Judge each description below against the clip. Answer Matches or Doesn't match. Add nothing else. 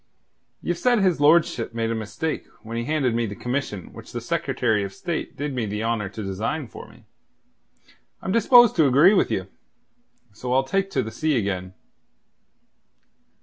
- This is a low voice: Matches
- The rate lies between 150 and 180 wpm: Matches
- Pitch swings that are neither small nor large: Doesn't match